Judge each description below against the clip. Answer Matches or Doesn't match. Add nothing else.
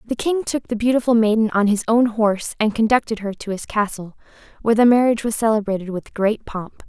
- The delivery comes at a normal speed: Doesn't match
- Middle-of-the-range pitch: Doesn't match